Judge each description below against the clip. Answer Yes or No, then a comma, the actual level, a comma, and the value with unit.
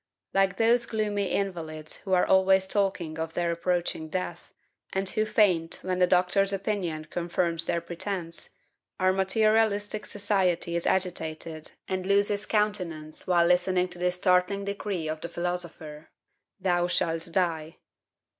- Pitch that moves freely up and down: No, average, 2.7 semitones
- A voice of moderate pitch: Yes, medium, 180 Hz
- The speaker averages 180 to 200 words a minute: No, slow, 135 wpm